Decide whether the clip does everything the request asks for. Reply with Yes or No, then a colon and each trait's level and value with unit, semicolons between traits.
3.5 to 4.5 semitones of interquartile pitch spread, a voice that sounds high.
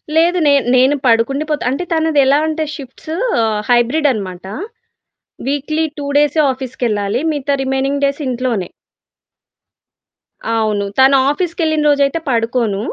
Yes: average, 4.0 semitones; very high, 275 Hz